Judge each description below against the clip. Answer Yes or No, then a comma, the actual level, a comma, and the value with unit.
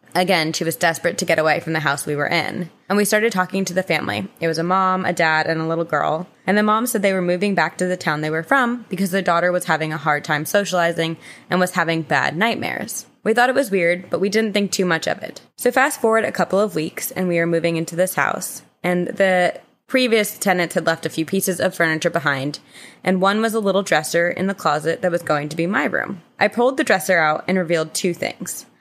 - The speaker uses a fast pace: Yes, fast, 255 wpm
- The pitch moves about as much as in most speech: Yes, average, 3.1 semitones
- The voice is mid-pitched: Yes, medium, 180 Hz